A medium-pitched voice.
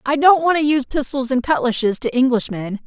No: very high, 260 Hz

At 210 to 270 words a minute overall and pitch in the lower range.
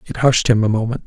No: fast, 280 wpm; low, 115 Hz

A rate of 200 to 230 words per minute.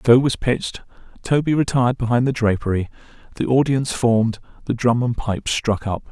No: average, 175 wpm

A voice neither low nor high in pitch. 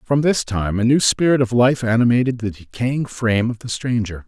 No: low, 120 Hz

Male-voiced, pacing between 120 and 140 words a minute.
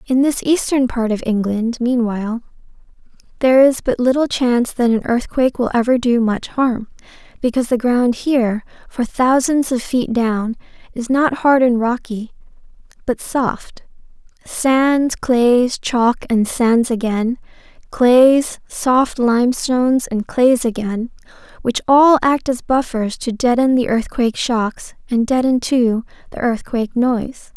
No: female; slow, 135 wpm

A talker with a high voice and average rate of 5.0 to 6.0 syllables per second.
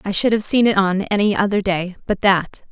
Yes: high, 200 Hz; 5.3 syllables/s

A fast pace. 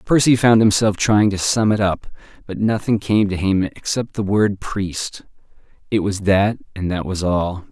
No: average, 185 wpm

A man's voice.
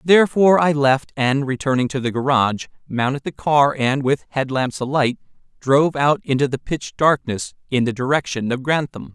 Yes: male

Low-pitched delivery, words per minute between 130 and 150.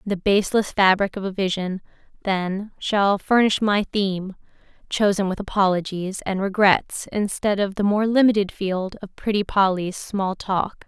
No: high, 195 Hz; average, 145 wpm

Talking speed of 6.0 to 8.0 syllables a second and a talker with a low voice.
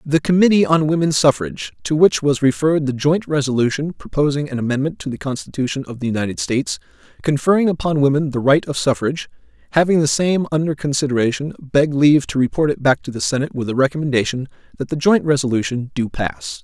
No: 6.3 syllables/s; medium, 145 Hz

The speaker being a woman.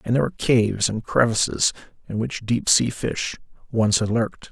No: male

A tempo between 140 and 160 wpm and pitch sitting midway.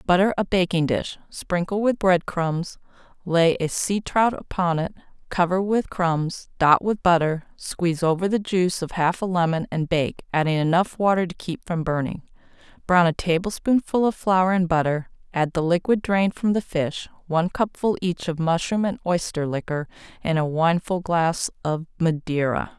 No: average, 170 wpm; medium, 175 Hz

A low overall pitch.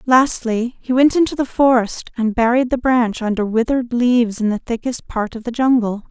No: high, 240 Hz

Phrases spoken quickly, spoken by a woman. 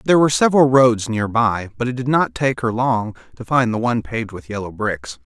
No: fast, 225 wpm; male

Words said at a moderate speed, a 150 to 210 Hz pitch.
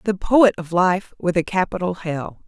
Yes: average, 195 wpm; medium, 185 Hz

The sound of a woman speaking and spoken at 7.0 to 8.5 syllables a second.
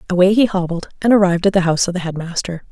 Yes: female; 7.6 syllables/s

